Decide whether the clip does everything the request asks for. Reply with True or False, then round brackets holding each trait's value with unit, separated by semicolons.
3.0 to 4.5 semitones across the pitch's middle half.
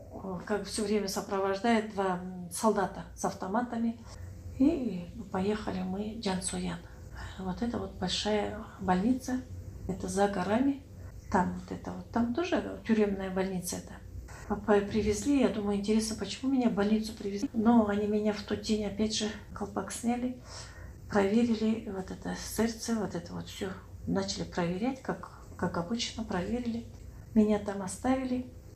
True (3.9 semitones)